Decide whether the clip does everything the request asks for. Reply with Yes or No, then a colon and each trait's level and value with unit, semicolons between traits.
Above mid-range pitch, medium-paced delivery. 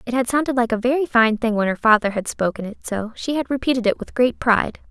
No: high, 240 Hz; fast, 270 wpm